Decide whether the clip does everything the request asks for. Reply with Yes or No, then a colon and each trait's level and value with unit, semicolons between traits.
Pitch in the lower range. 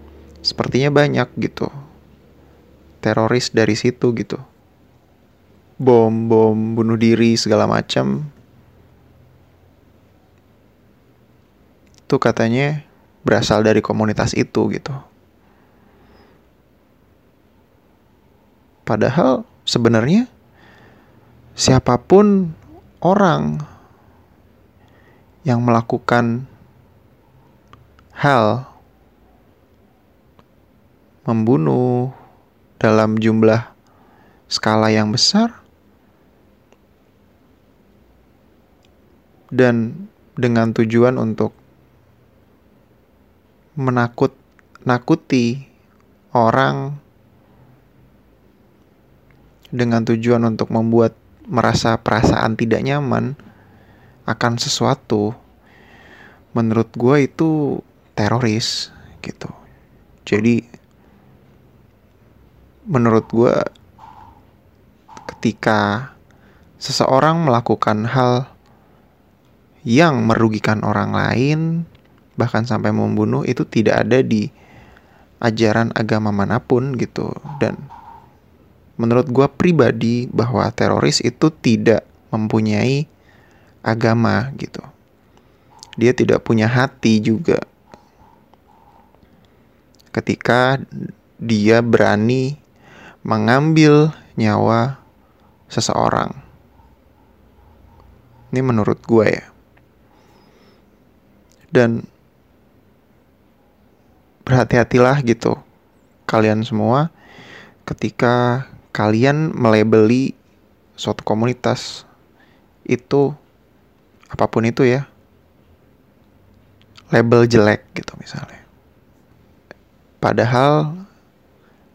Yes: low, 115 Hz